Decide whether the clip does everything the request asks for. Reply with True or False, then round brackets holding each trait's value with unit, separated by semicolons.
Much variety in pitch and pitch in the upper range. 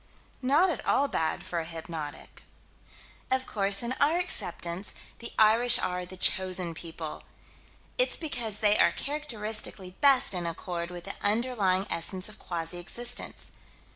True (5.8 semitones; 195 Hz)